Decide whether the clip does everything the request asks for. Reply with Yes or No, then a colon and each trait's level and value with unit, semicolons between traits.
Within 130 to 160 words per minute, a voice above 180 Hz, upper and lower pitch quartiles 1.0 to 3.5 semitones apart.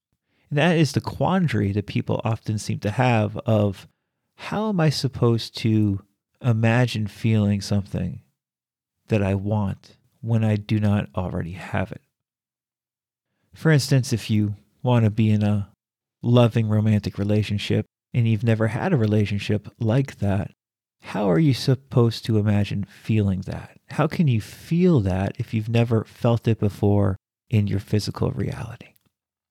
No: average, 150 wpm; low, 110 Hz; average, 3.0 semitones